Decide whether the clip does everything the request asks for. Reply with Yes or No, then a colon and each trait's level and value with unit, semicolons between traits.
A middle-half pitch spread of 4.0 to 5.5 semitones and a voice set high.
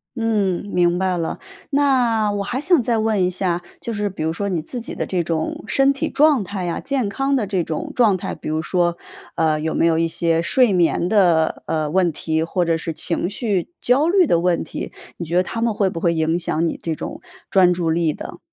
No: average, 5.1 semitones; medium, 180 Hz